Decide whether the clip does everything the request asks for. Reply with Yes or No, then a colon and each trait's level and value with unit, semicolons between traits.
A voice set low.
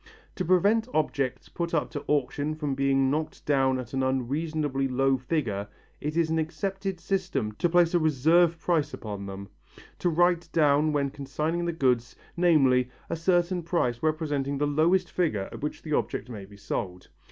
No: medium, 150 Hz